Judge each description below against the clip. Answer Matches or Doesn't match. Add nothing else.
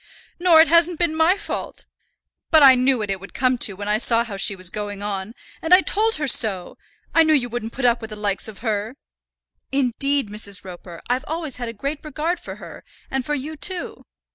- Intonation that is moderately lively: Doesn't match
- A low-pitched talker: Doesn't match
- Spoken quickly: Matches